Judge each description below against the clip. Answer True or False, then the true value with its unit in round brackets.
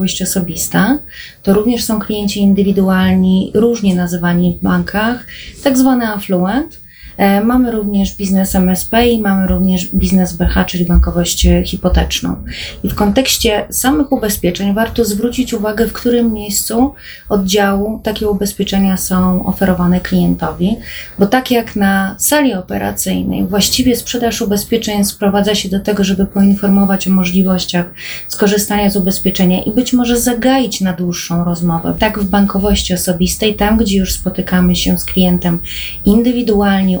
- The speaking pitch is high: True (200 Hz)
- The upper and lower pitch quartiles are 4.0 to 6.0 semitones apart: False (3.0 semitones)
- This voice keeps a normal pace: True (130 wpm)